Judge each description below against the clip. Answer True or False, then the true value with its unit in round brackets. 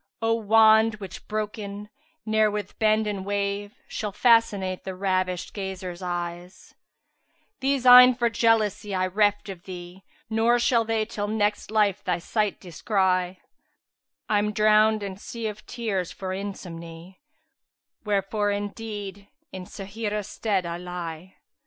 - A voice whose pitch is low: False (205 Hz)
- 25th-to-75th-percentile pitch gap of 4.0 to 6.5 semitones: False (2.6 semitones)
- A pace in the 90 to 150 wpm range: True (140 wpm)